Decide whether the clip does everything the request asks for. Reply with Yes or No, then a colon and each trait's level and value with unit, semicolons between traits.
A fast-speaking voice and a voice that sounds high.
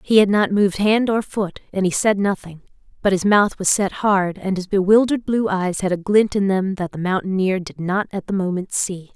Yes: fast, 235 wpm; high, 195 Hz